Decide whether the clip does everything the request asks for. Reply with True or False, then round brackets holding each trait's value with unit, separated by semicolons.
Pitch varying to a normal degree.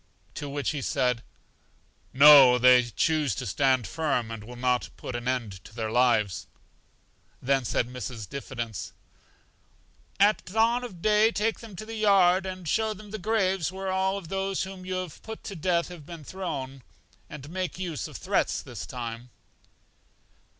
False (7.4 semitones)